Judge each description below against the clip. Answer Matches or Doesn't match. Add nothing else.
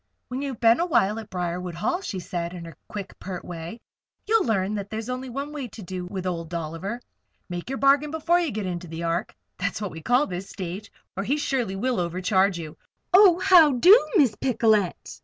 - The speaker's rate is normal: Doesn't match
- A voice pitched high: Matches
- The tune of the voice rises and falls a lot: Matches